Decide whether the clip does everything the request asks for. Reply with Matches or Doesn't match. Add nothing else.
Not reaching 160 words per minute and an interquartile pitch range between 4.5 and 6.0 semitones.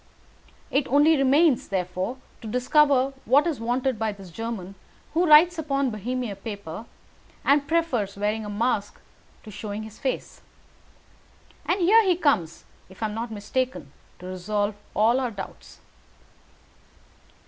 Matches